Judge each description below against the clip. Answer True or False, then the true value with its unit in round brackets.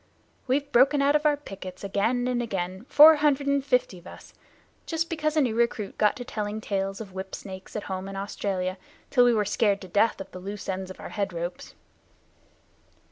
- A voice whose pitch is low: False (210 Hz)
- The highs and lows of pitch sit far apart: True (5.9 semitones)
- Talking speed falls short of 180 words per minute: False (205 wpm)